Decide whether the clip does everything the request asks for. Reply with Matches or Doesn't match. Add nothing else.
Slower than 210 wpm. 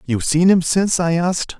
Doesn't match